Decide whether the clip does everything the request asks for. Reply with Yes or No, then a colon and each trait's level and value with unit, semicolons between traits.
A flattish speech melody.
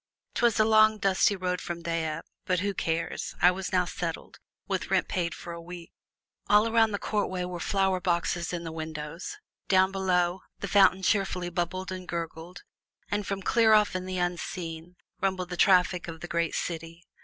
Yes: narrow, 2.3 semitones